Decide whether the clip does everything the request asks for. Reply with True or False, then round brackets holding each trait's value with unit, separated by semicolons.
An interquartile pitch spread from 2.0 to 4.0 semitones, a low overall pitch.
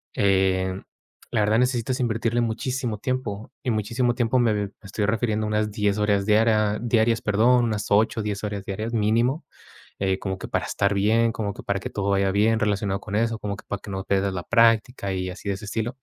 True (2.4 semitones; 105 Hz)